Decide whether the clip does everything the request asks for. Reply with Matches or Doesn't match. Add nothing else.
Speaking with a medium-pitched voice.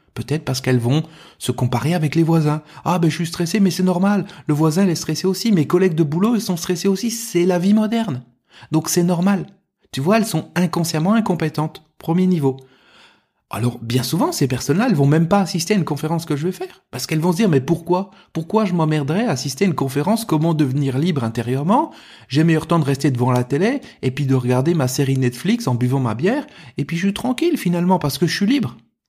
Matches